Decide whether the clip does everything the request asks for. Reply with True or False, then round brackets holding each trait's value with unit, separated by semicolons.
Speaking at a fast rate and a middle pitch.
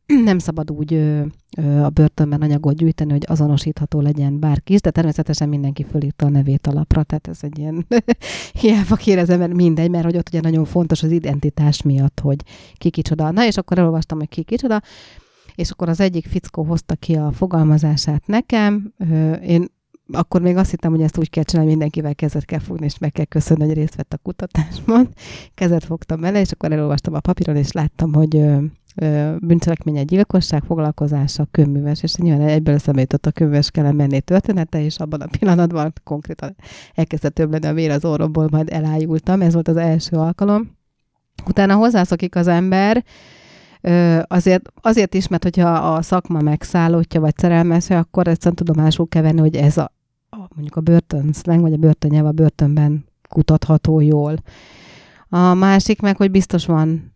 True (175 wpm; 160 Hz)